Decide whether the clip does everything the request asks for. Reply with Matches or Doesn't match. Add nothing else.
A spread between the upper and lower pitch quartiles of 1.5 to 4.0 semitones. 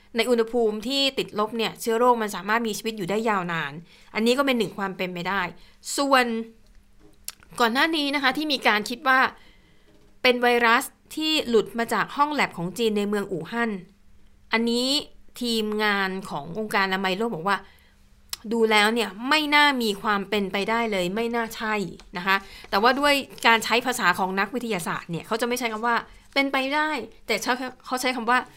Matches